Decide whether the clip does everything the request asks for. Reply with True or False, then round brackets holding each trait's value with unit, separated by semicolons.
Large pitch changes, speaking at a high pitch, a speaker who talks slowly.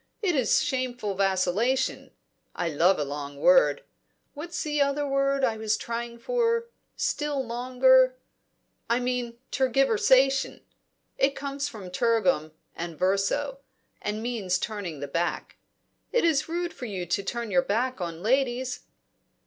True (5.9 semitones; 245 Hz; 130 wpm)